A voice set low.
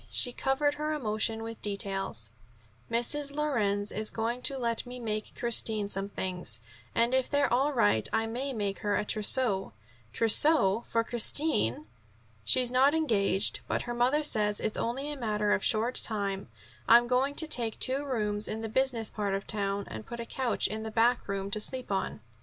No: high, 225 Hz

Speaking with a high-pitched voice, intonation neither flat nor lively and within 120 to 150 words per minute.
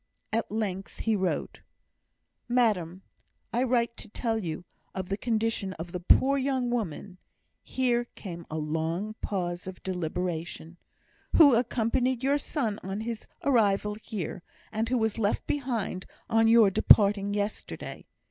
Yes: high, 215 Hz; average, 4.3 semitones; average, 140 wpm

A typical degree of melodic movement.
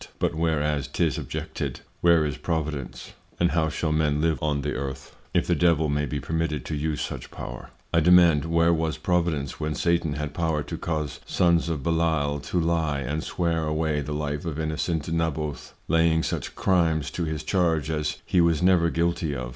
No: narrow, 2.0 semitones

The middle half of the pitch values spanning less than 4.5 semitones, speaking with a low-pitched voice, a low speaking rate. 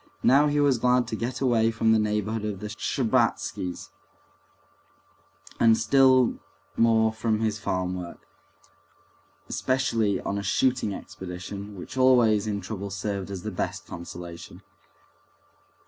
Yes: average, 3.4 semitones; low, 110 Hz; slow, 130 wpm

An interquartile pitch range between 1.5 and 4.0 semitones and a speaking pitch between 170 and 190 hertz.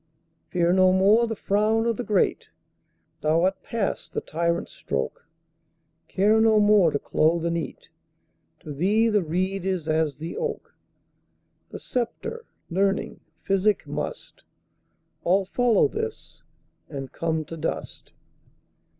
No: average, 4.7 semitones; medium, 185 Hz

